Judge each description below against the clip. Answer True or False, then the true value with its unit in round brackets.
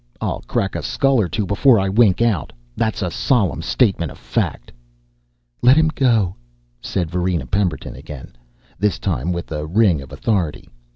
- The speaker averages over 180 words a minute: False (165 wpm)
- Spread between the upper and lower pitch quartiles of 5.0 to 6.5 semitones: True (5.3 semitones)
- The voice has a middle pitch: False (95 Hz)